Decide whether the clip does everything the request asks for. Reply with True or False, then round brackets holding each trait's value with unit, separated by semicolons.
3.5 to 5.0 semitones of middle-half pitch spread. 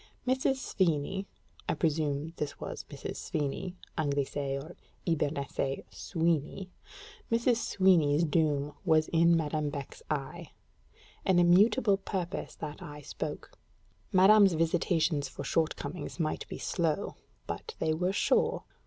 True (4.1 semitones)